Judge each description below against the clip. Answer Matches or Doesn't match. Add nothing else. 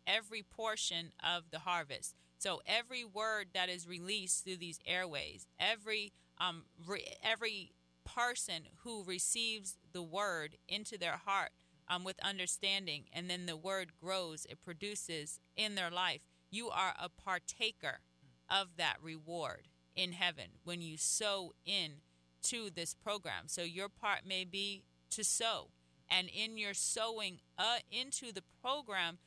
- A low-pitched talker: Doesn't match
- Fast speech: Doesn't match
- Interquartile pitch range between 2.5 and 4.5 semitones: Matches